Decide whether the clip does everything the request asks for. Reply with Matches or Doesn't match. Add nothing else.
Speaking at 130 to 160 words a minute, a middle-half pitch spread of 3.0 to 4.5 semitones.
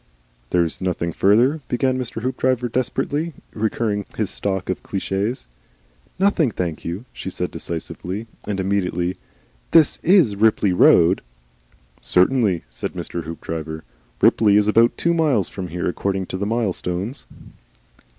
Doesn't match